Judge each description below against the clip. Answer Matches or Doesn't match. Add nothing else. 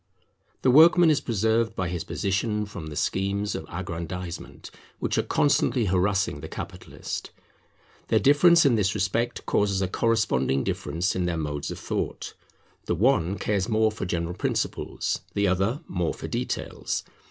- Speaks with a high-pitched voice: Doesn't match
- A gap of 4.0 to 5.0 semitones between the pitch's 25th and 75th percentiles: Matches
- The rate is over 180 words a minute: Doesn't match